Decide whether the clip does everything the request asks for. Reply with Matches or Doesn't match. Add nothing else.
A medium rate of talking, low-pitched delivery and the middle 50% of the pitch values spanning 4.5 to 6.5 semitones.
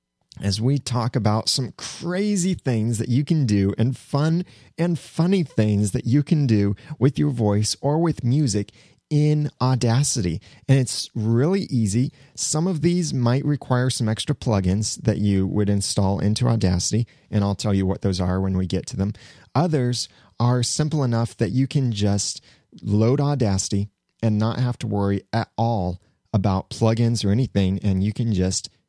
Matches